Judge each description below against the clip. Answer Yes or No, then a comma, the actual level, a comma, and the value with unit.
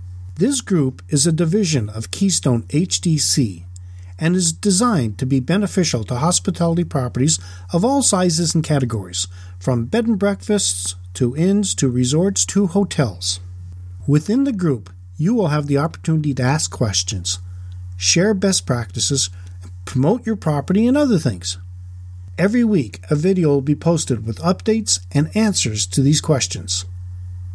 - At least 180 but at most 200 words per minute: No, average, 145 wpm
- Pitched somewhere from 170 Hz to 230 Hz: No, medium, 140 Hz